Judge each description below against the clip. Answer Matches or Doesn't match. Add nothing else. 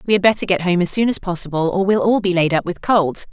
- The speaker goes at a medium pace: Doesn't match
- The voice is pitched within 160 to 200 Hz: Matches